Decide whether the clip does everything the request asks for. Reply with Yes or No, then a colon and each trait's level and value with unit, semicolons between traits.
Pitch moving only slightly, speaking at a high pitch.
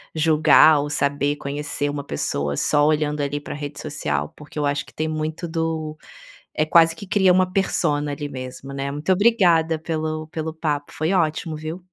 No: narrow, 2.0 semitones; medium, 155 Hz